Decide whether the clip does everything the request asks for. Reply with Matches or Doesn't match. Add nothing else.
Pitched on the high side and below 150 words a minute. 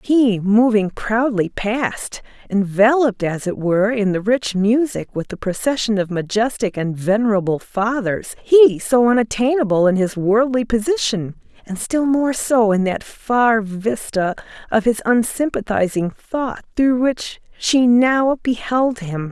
Matches